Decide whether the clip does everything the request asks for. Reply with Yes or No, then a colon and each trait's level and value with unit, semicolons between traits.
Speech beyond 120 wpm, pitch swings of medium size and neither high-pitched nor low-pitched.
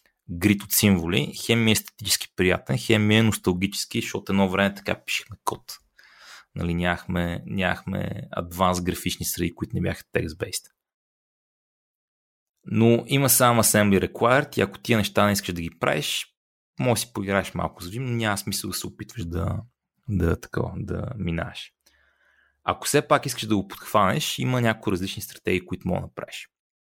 No: average, 160 wpm; average, 3.6 semitones; low, 100 Hz